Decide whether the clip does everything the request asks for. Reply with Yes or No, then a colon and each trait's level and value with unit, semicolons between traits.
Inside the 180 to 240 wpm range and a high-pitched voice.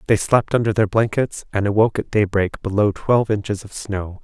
No: average, 200 wpm; low, 105 Hz